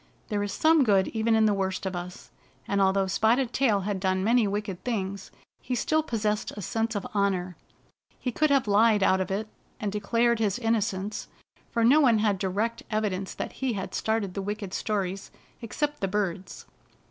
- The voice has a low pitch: No, high, 210 Hz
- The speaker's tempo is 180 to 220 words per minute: Yes, average, 190 wpm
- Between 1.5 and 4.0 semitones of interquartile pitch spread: Yes, average, 2.9 semitones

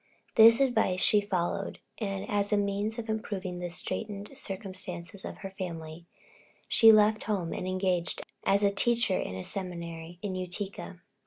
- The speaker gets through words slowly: No, average, 155 wpm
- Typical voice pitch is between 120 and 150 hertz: No, high, 195 Hz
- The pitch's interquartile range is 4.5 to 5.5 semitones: No, average, 2.7 semitones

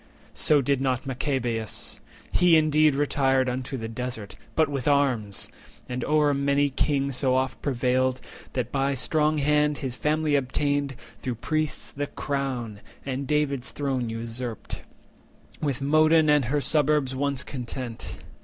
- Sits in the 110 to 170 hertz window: Yes, low, 135 Hz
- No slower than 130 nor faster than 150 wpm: Yes, average, 140 wpm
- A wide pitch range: No, narrow, 2.5 semitones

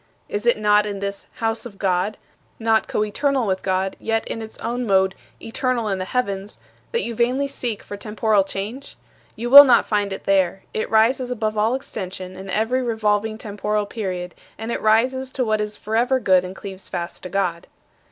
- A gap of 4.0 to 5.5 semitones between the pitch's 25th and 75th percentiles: No, average, 3.3 semitones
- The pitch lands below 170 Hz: No, high, 215 Hz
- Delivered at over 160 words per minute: Yes, average, 190 wpm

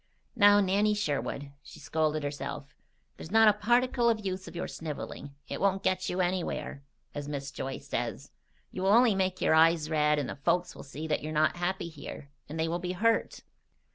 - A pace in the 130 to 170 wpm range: No, average, 195 wpm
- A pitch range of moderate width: Yes, average, 4.7 semitones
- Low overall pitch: No, medium, 175 Hz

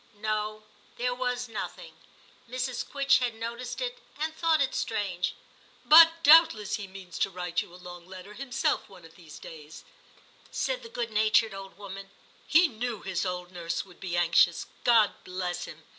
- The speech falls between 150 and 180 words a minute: Yes, average, 175 wpm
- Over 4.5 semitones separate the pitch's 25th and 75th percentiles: Yes, wide, 5.6 semitones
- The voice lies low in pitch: No, high, 215 Hz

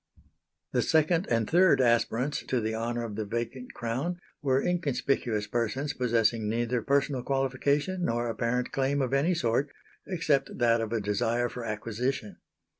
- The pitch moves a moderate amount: Yes, average, 3.3 semitones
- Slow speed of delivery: No, average, 150 wpm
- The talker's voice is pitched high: No, low, 125 Hz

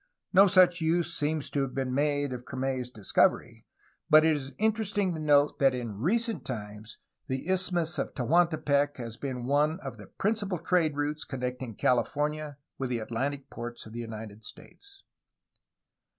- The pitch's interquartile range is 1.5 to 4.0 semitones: No, average, 5.1 semitones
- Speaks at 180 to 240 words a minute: No, average, 160 wpm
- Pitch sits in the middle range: Yes, medium, 145 Hz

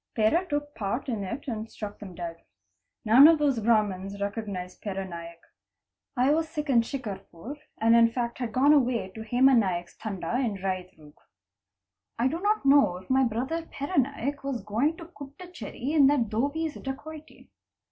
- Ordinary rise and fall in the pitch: No, wide, 5.9 semitones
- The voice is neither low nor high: No, high, 235 Hz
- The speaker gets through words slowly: No, average, 170 wpm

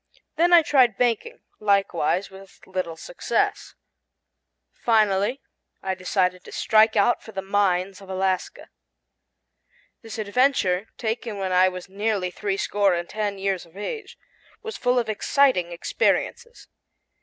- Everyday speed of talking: No, slow, 130 wpm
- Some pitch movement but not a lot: Yes, average, 3.5 semitones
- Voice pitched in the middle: No, high, 200 Hz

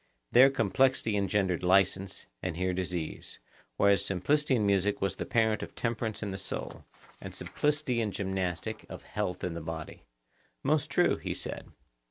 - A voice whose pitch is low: Yes, low, 100 Hz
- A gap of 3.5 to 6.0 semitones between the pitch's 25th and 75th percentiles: Yes, average, 4.2 semitones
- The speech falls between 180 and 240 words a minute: No, average, 160 wpm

